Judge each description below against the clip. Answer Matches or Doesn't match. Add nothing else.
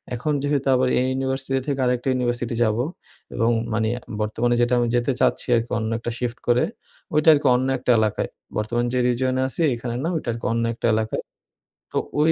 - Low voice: Matches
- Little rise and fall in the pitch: Matches